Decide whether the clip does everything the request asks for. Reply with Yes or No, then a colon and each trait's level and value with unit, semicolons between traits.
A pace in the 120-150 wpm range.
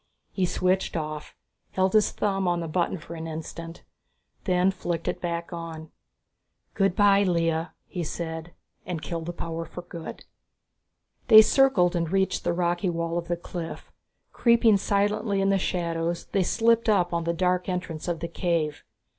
No: average, 165 wpm